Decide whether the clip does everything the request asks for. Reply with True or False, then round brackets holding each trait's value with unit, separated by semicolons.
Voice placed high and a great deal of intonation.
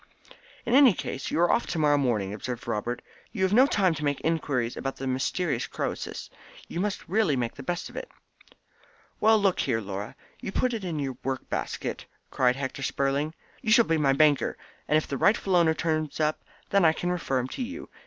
False (155 Hz; 5.9 semitones)